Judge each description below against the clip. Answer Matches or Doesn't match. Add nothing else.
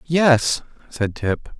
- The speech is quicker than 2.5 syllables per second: Doesn't match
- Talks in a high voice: Doesn't match